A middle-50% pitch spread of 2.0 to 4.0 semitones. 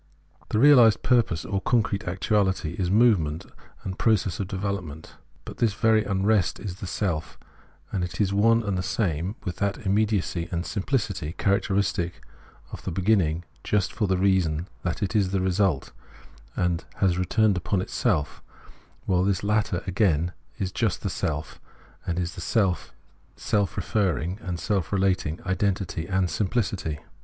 Yes: average, 2.8 semitones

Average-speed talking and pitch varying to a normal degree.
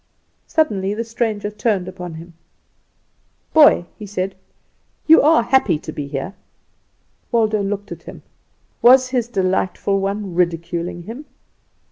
No: slow, 125 wpm; average, 4.5 semitones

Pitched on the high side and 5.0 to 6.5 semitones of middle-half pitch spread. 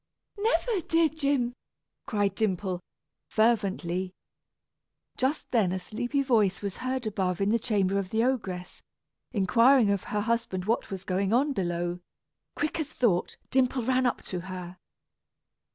Yes: high, 215 Hz; wide, 5.4 semitones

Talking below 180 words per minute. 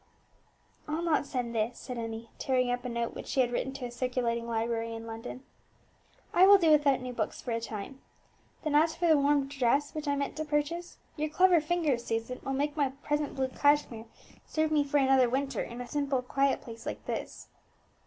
No: fast, 205 wpm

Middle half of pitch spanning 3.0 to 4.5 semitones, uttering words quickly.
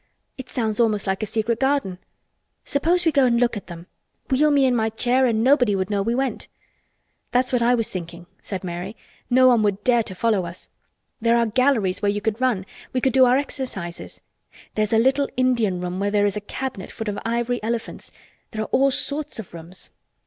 Yes: average, 4.1 semitones; fast, 215 wpm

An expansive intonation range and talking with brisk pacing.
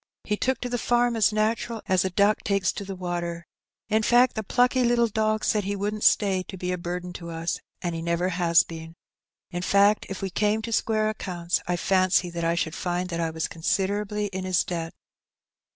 No: average, 3.7 semitones; fast, 215 wpm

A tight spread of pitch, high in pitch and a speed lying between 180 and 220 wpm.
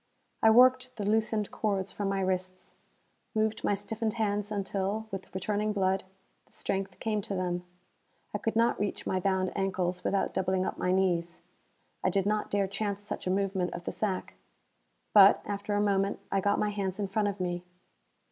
Yes: narrow, 1.8 semitones; high, 200 Hz; average, 185 wpm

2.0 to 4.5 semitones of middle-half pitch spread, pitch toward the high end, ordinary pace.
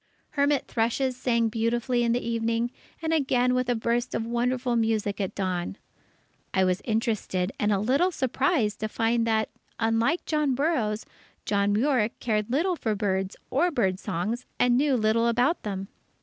Yes: average, 3.1 semitones; high, 230 Hz; average, 165 wpm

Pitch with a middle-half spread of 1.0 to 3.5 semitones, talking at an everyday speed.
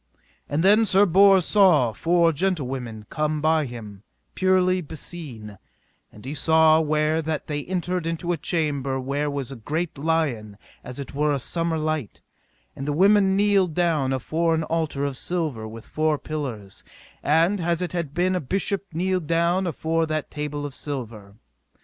No: average, 3.9 semitones; average, 160 wpm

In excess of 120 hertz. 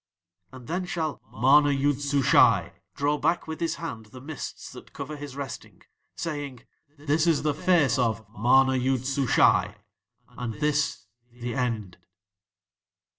Yes: medium, 140 Hz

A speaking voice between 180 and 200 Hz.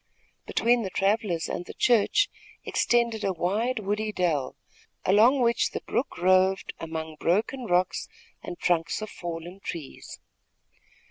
Yes: high, 190 Hz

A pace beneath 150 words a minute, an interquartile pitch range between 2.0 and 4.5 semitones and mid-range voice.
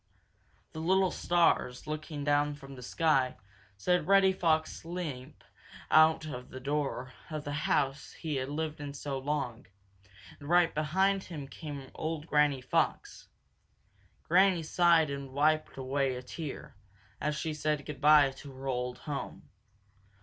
Yes: average, 140 wpm; average, 2.7 semitones; medium, 150 Hz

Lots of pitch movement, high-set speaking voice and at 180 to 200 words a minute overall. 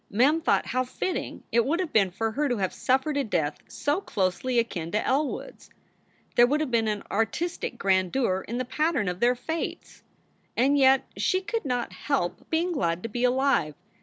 Yes: wide, 5.8 semitones; high, 245 Hz; average, 195 wpm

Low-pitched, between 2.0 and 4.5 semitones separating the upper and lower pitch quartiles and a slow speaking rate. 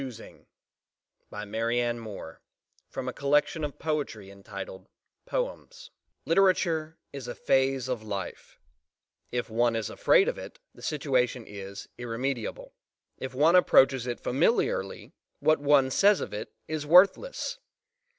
No: low, 130 Hz; average, 5.2 semitones; slow, 115 wpm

